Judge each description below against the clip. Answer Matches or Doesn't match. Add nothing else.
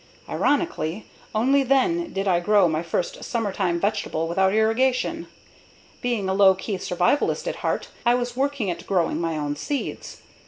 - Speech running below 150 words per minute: Doesn't match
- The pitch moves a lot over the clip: Matches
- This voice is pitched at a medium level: Doesn't match